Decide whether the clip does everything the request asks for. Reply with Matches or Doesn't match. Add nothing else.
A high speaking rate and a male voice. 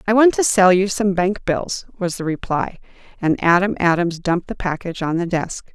Doesn't match